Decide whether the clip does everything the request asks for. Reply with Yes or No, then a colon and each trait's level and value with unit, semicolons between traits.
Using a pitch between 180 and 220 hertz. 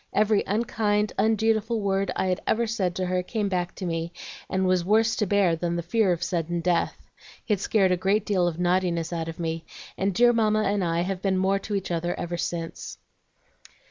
Yes: medium, 185 Hz